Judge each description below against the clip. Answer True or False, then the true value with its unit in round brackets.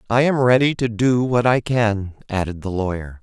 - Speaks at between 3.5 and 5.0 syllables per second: True (4.8 syllables/s)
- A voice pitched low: True (115 Hz)